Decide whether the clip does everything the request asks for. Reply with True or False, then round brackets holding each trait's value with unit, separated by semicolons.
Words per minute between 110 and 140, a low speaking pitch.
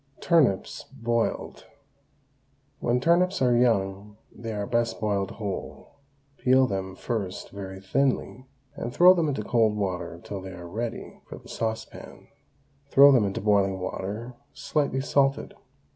True (135 wpm; 115 Hz)